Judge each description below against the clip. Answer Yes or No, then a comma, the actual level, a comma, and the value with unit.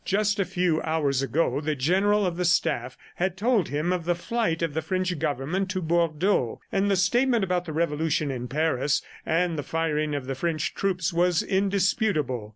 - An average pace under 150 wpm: No, average, 185 wpm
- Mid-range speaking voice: Yes, medium, 170 Hz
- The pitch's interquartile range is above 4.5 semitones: No, average, 4.0 semitones